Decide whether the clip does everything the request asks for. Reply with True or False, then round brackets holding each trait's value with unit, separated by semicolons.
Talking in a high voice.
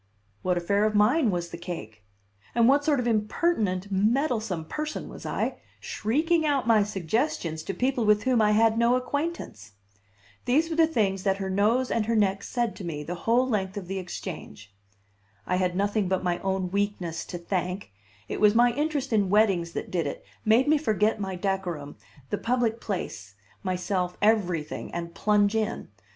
True (205 Hz)